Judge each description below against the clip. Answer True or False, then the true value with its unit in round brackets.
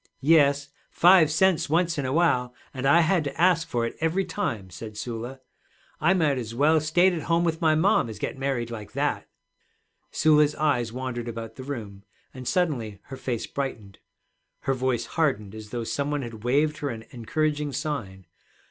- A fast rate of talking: False (185 wpm)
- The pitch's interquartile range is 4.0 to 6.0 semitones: True (5.0 semitones)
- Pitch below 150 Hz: True (140 Hz)